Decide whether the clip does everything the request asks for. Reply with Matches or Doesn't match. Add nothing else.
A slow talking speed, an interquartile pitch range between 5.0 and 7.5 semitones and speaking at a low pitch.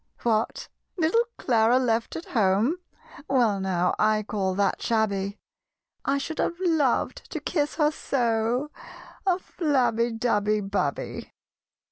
Doesn't match